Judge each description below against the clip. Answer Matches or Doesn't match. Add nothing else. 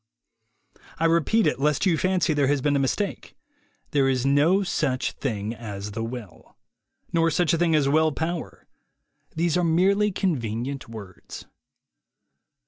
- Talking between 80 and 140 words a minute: Doesn't match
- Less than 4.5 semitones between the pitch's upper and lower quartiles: Doesn't match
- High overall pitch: Doesn't match